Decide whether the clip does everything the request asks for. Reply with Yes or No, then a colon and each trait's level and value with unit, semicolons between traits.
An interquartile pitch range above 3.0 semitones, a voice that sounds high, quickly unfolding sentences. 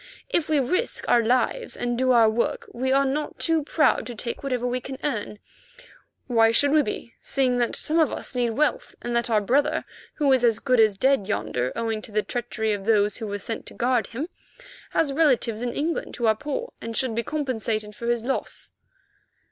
Yes: average, 3.7 semitones; high, 245 Hz; fast, 210 wpm